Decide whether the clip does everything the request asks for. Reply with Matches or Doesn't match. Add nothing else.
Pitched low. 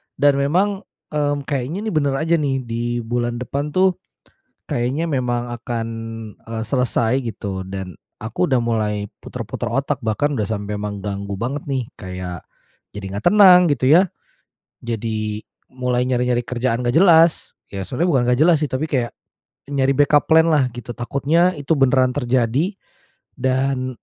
Matches